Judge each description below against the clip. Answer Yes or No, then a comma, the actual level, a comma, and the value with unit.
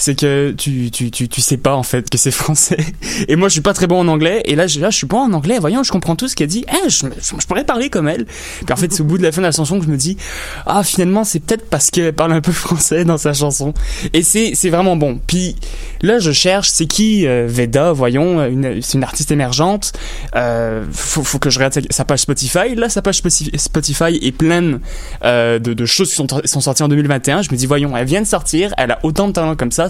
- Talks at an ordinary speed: No, fast, 265 wpm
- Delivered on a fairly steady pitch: No, average, 4.5 semitones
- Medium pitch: Yes, medium, 155 Hz